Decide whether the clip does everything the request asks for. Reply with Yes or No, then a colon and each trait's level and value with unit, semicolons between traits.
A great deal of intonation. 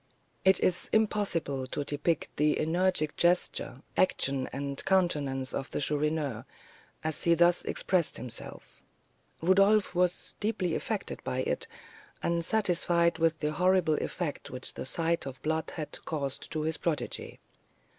No: average, 3.6 semitones